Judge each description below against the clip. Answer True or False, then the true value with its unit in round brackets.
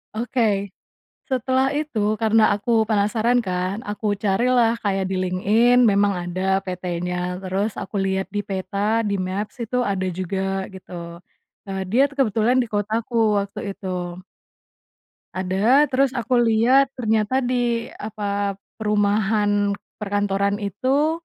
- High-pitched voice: True (210 Hz)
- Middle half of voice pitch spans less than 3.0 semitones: False (3.5 semitones)